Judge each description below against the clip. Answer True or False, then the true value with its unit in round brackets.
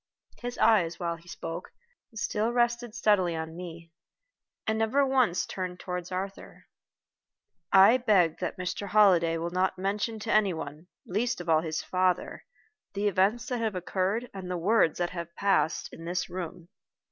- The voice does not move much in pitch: False (4.0 semitones)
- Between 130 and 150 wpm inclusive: False (165 wpm)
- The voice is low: False (185 Hz)